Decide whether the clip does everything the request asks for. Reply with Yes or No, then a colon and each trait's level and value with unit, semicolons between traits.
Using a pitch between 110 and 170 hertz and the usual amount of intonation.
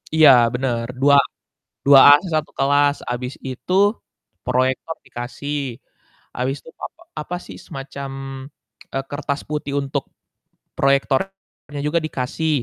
No: medium, 140 Hz; narrow, 2.0 semitones